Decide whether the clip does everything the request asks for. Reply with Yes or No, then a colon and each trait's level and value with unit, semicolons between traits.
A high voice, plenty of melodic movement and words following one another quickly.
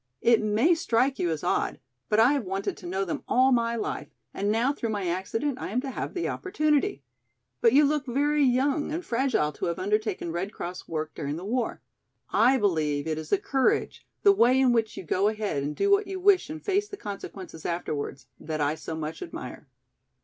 Yes: high, 225 Hz; wide, 8.0 semitones; fast, 210 wpm